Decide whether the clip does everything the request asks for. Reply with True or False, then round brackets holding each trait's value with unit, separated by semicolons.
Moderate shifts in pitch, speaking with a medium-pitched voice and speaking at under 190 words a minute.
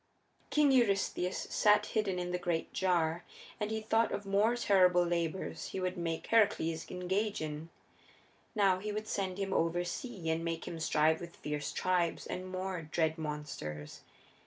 True (3.6 semitones; 180 Hz; 160 wpm)